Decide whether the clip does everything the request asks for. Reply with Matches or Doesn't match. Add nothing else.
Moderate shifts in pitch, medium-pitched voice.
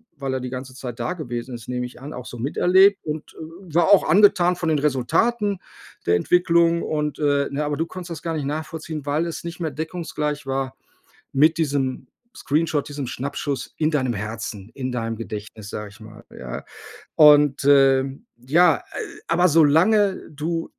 Matches